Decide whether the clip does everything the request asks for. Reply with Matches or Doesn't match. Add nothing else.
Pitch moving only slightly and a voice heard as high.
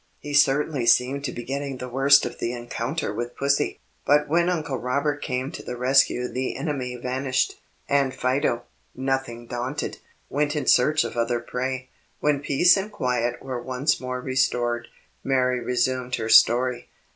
Doesn't match